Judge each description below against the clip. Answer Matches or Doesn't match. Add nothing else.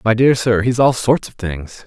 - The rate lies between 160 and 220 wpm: Doesn't match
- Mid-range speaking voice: Doesn't match